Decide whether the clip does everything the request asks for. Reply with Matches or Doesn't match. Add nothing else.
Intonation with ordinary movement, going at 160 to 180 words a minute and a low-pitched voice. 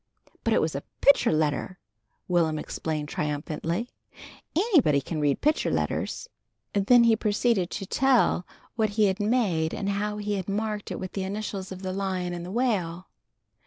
Doesn't match